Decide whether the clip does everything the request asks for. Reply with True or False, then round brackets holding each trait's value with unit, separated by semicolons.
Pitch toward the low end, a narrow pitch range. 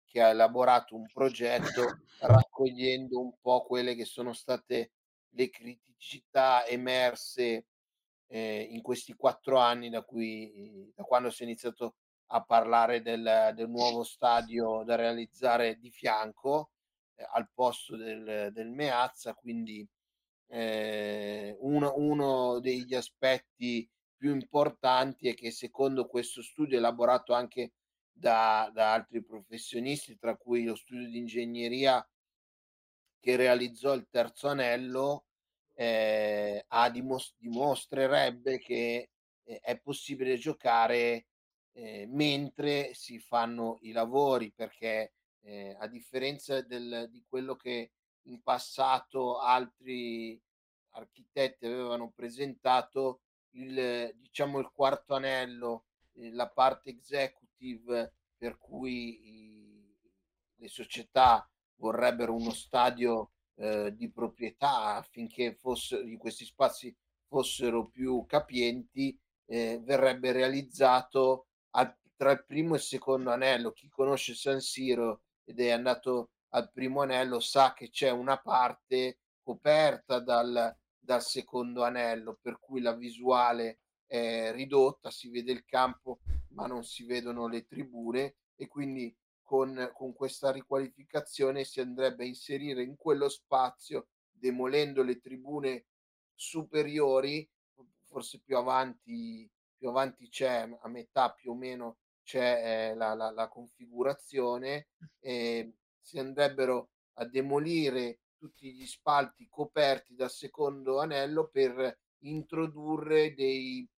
True (125 Hz; 2.3 semitones)